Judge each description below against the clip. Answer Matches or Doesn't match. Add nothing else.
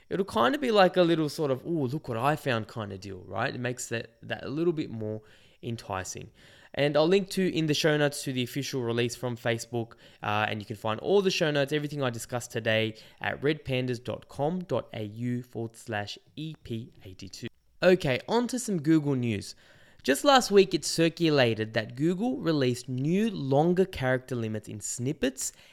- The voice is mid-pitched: Doesn't match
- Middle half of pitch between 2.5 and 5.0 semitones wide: Doesn't match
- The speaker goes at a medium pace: Matches